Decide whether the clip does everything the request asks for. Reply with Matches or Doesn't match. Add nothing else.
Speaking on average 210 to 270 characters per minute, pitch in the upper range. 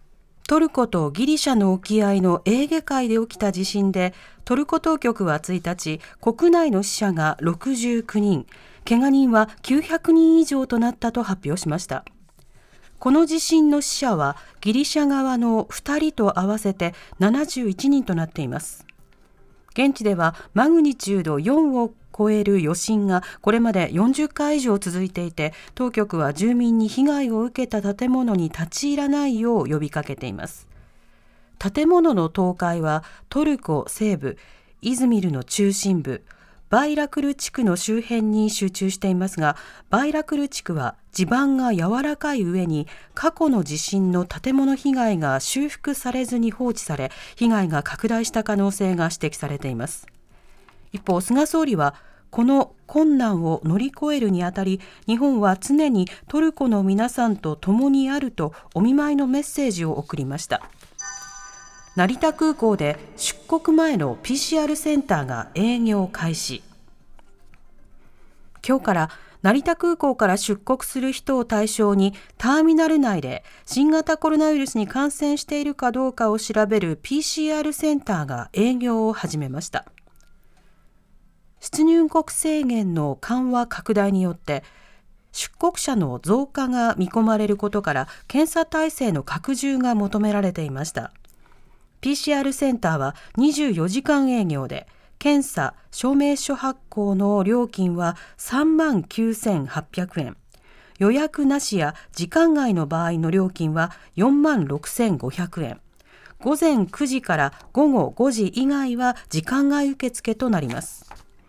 Matches